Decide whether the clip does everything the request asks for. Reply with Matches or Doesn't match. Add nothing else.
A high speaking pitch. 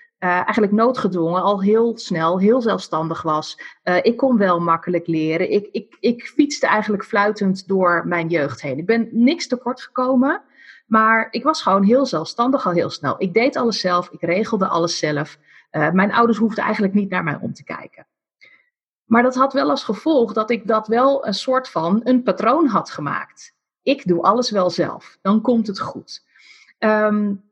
Matches